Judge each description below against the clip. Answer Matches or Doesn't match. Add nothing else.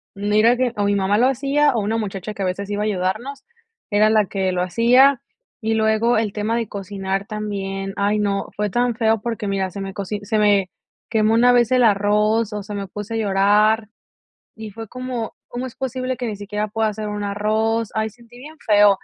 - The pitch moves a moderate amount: Doesn't match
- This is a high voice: Matches